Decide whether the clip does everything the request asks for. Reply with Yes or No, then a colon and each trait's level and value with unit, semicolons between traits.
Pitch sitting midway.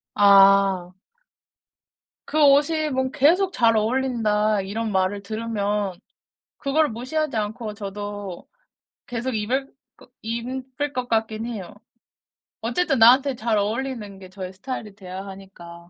No: high, 220 Hz